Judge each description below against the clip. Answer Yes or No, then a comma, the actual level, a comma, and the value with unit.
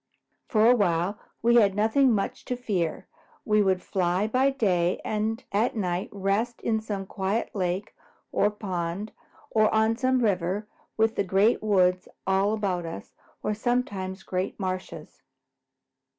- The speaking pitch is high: Yes, high, 205 Hz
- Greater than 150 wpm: No, average, 145 wpm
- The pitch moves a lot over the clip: No, average, 3.0 semitones